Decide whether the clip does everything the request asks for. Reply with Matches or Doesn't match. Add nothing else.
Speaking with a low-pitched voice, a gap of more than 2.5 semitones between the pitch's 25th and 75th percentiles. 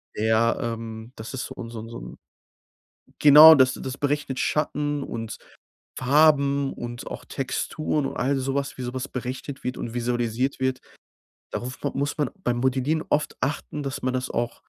Matches